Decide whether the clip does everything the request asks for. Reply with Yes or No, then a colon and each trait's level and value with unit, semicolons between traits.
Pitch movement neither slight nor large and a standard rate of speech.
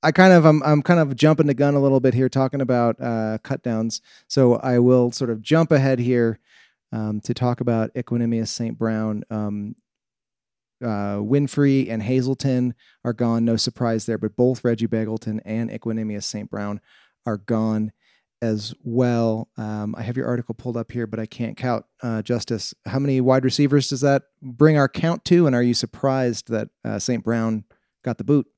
Yes: average, 3.1 semitones; average, 190 wpm